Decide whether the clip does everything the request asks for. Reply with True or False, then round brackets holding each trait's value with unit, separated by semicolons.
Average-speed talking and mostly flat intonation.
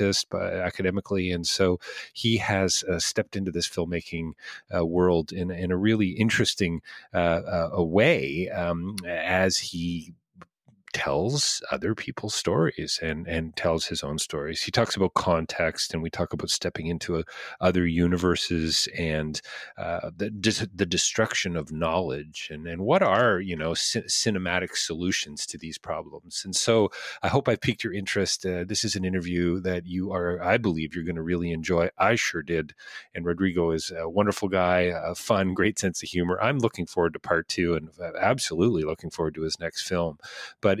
True (175 wpm; 2.3 semitones)